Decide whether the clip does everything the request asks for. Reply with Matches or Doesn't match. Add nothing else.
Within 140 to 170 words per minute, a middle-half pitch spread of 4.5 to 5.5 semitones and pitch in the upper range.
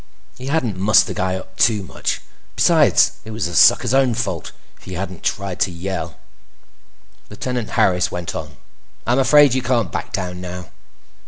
Doesn't match